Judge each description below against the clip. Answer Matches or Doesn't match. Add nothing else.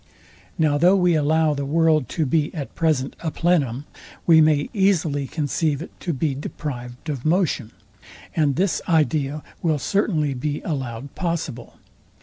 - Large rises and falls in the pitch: Doesn't match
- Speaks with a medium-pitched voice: Matches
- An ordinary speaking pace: Matches